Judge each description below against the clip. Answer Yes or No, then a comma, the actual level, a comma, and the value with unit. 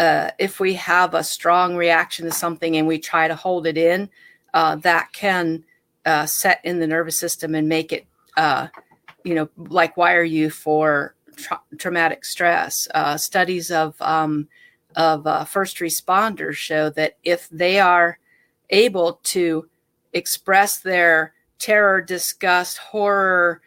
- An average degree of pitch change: No, narrow, 2.3 semitones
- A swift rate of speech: No, average, 150 wpm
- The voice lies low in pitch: No, medium, 170 Hz